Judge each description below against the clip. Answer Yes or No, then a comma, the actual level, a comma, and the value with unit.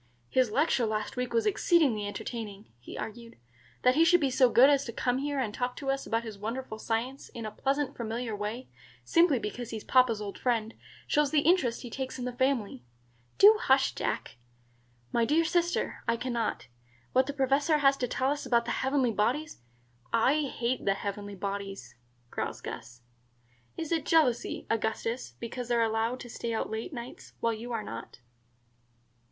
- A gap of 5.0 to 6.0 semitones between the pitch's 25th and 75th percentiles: No, average, 3.7 semitones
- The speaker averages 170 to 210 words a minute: Yes, average, 185 wpm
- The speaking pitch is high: Yes, high, 245 Hz